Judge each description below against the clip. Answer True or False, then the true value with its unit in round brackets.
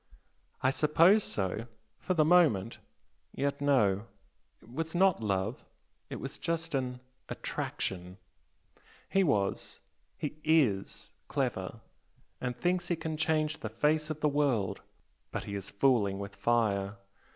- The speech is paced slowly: True (130 wpm)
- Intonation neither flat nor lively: False (7.5 semitones)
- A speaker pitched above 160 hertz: False (135 Hz)